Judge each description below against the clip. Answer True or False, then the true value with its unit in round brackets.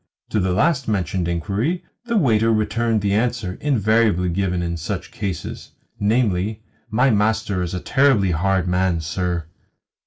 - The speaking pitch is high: False (100 Hz)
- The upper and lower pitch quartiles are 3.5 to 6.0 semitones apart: True (3.9 semitones)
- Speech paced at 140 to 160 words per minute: True (145 wpm)